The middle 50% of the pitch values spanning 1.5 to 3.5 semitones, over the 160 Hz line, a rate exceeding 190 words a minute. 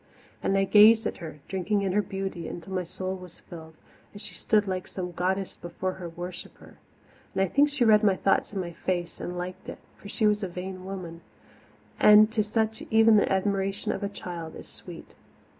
Yes: narrow, 2.6 semitones; high, 190 Hz; average, 200 wpm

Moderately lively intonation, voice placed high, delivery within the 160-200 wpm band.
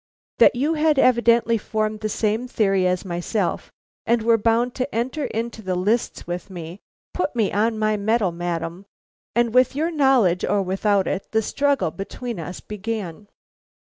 Yes: average, 4.0 semitones; high, 215 Hz; average, 165 wpm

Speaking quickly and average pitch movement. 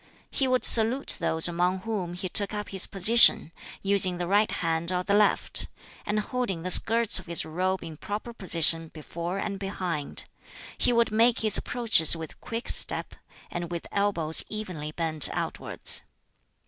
No: average, 160 wpm; average, 4.1 semitones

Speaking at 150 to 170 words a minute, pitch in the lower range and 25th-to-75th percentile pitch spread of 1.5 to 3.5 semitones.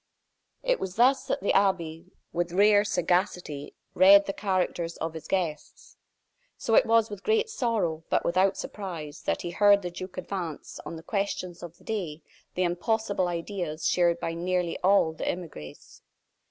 No: average, 165 wpm; medium, 180 Hz; average, 3.1 semitones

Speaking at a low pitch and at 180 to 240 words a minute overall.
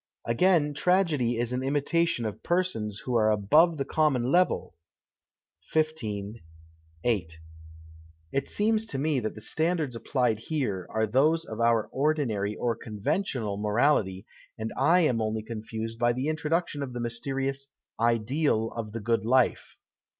No: low, 125 Hz; average, 145 wpm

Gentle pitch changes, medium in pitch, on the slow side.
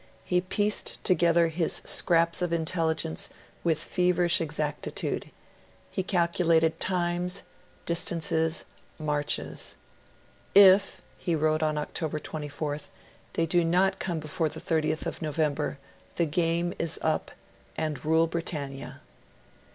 Yes: narrow, 2.1 semitones; medium, 165 Hz; slow, 105 wpm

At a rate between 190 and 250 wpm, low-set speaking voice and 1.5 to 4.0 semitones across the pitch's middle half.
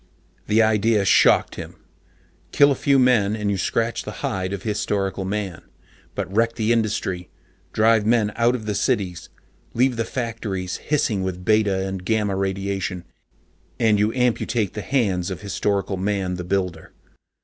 No: average, 155 wpm; low, 105 Hz; average, 3.0 semitones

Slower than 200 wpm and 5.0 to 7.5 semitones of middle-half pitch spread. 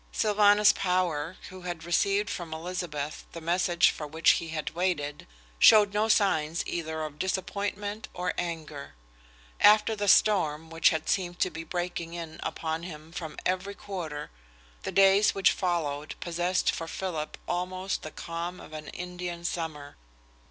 No: average, 150 wpm; average, 2.9 semitones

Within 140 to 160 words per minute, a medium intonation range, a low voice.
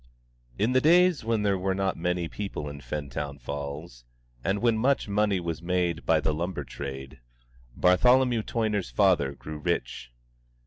No: average, 150 wpm; wide, 6.4 semitones; very low, 90 Hz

